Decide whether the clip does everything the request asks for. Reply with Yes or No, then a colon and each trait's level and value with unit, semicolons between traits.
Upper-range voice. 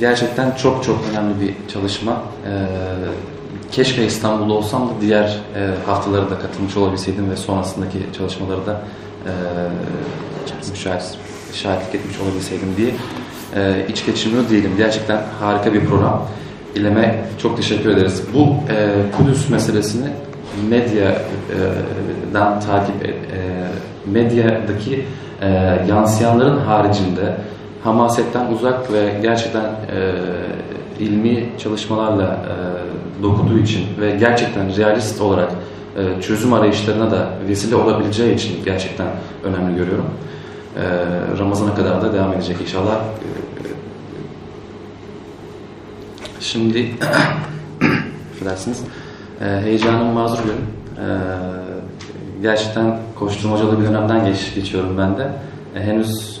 No: low, 105 Hz